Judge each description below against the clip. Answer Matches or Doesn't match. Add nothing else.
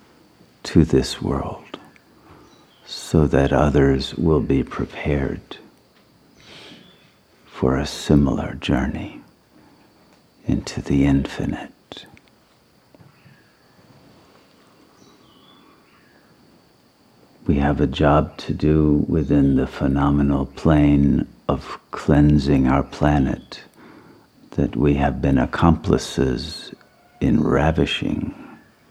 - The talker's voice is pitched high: Doesn't match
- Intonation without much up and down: Matches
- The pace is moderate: Doesn't match